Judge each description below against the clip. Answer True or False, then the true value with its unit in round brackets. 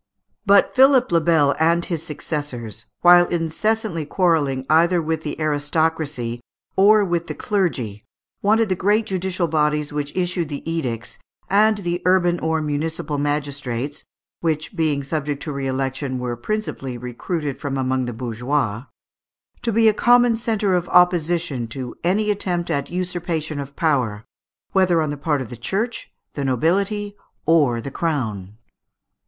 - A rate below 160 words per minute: True (150 wpm)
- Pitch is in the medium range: True (160 Hz)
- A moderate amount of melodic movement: True (4.6 semitones)